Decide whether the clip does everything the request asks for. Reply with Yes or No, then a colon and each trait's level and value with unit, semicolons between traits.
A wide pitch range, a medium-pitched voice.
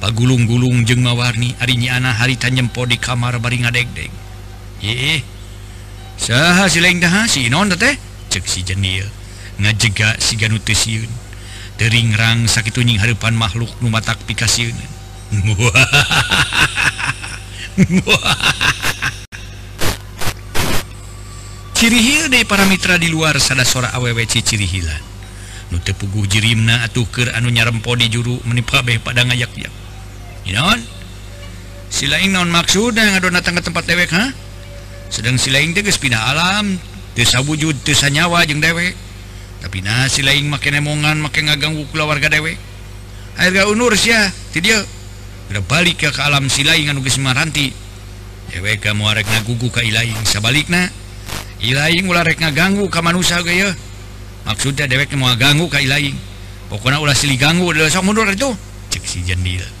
No: wide, 6.9 semitones; low, 120 Hz